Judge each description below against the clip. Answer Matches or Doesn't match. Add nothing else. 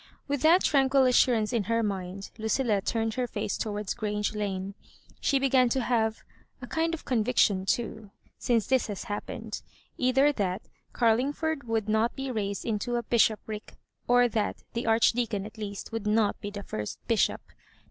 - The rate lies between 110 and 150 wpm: Doesn't match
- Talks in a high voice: Matches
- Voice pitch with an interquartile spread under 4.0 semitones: Matches